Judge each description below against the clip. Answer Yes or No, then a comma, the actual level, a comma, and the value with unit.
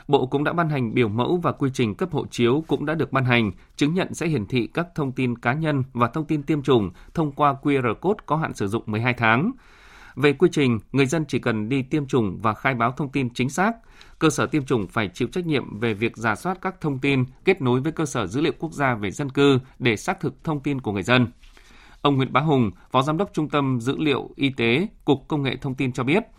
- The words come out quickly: Yes, fast, 260 wpm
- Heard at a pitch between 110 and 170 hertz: Yes, medium, 140 Hz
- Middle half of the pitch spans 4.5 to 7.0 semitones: No, average, 4.0 semitones